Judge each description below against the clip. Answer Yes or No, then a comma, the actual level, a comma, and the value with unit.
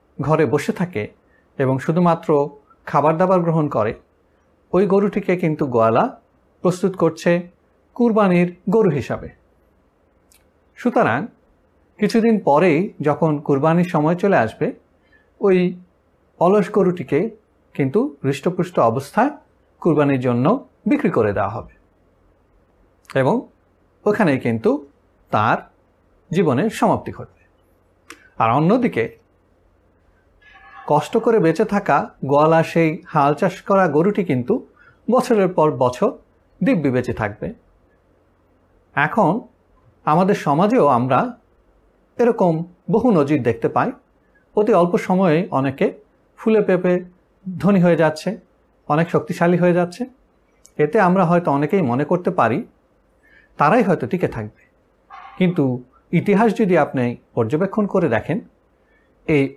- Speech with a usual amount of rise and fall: No, wide, 8.5 semitones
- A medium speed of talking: Yes, average, 105 wpm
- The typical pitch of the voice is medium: Yes, medium, 155 Hz